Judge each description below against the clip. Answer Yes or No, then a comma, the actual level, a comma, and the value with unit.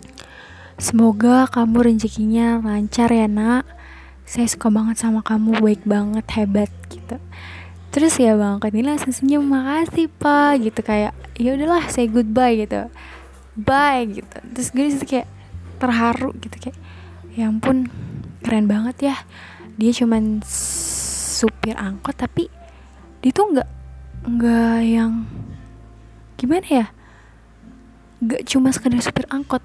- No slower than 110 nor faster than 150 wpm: Yes, average, 125 wpm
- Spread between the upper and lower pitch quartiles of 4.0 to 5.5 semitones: Yes, average, 4.7 semitones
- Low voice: No, high, 225 Hz